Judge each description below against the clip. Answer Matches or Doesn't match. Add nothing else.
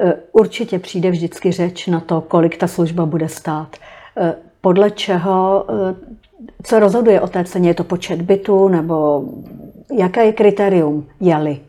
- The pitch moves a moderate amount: Matches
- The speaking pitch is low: Doesn't match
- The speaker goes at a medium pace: Matches